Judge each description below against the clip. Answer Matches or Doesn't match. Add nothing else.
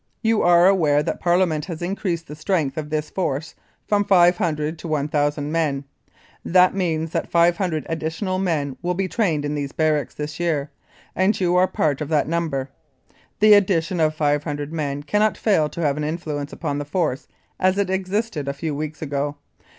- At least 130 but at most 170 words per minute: Doesn't match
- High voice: Doesn't match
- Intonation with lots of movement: Doesn't match